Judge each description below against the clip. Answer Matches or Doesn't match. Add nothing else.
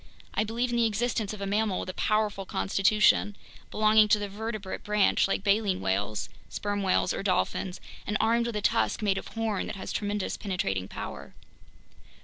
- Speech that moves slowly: Doesn't match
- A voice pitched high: Matches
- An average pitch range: Doesn't match